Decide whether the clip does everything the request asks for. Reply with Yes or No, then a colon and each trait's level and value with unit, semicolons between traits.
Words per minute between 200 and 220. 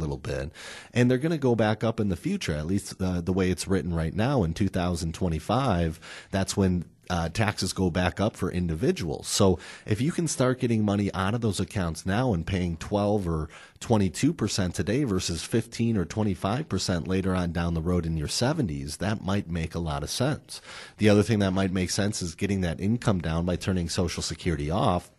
Yes: fast, 205 wpm